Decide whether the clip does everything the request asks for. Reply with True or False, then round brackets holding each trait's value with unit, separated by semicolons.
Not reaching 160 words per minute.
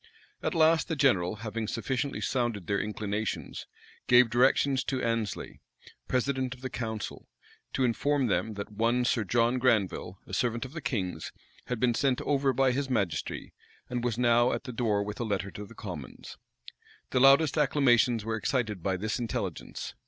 False (170 wpm)